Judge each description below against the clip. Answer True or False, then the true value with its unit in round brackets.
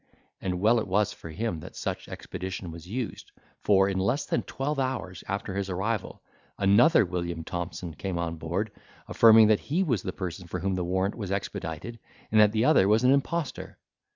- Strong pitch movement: False (4.0 semitones)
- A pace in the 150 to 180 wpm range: False (190 wpm)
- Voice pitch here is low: True (100 Hz)